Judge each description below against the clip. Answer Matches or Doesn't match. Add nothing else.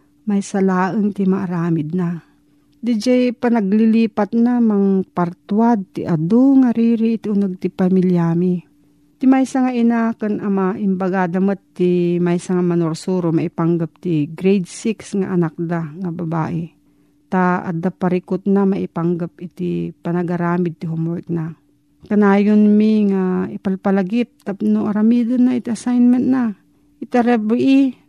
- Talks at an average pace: Matches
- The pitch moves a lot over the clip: Doesn't match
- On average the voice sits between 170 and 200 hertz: Matches